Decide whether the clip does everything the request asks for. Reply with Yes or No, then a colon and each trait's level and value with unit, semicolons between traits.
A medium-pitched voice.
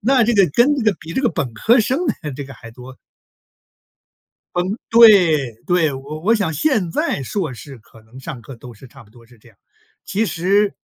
Yes: medium, 160 Hz